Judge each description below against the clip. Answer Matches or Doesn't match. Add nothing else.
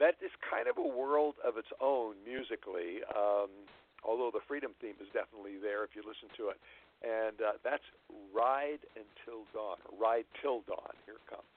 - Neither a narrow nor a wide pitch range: Doesn't match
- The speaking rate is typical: Matches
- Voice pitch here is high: Doesn't match